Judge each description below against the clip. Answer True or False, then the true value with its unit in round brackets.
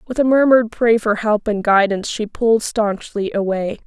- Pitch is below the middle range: False (220 Hz)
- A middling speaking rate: True (185 wpm)